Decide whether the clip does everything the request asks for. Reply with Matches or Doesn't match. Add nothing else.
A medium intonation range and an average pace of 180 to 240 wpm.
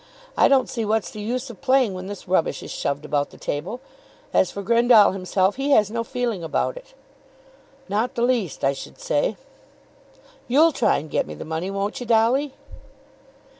Matches